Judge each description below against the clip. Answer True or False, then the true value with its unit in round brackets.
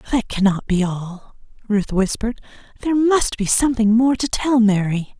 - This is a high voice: True (225 Hz)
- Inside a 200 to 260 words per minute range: False (160 wpm)